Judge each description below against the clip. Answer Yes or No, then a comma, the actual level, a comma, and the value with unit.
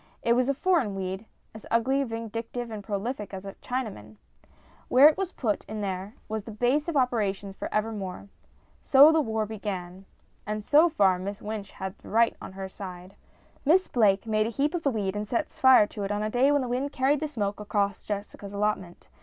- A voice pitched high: Yes, high, 215 Hz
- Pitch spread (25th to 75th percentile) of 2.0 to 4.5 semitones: Yes, average, 4.2 semitones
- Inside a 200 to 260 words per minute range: Yes, fast, 205 wpm